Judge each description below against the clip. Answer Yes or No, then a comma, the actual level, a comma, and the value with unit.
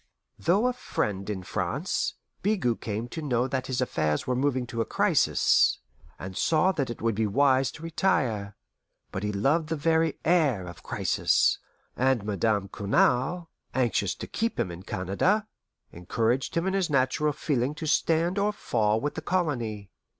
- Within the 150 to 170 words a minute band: Yes, average, 165 wpm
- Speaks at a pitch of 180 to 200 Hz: No, low, 130 Hz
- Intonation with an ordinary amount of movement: No, wide, 7.5 semitones